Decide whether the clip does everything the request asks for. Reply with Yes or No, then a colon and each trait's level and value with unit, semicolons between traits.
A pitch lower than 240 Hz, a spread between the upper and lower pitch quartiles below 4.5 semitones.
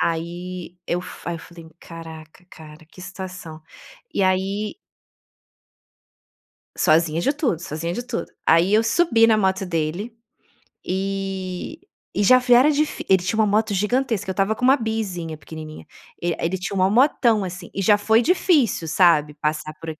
No: high, 190 Hz; average, 4.8 semitones